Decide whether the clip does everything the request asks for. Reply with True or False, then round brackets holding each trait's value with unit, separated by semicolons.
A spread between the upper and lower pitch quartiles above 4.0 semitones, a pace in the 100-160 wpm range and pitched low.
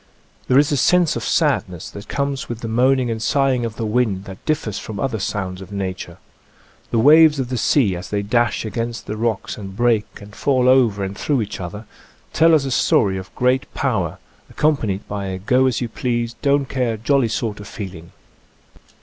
False (4.5 semitones; 200 wpm; 115 Hz)